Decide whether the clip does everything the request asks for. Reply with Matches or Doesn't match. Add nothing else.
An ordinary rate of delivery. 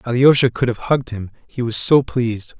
Doesn't match